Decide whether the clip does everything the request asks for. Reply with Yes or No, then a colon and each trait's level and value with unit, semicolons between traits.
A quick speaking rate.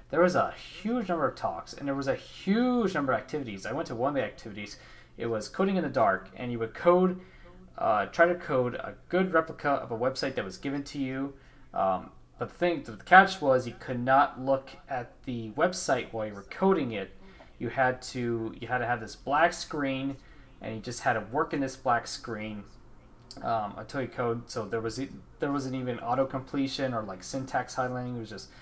Yes: fast, 220 wpm